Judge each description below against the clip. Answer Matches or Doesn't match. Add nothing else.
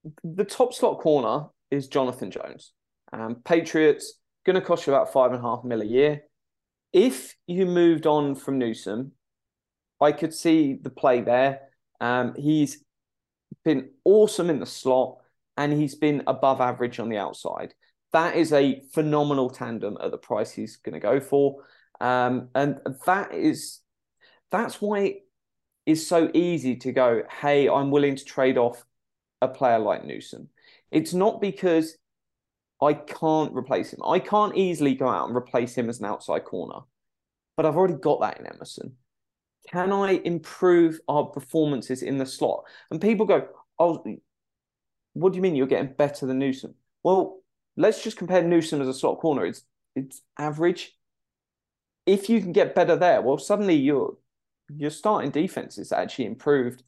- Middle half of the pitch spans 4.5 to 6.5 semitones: Matches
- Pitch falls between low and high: Matches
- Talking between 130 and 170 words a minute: Matches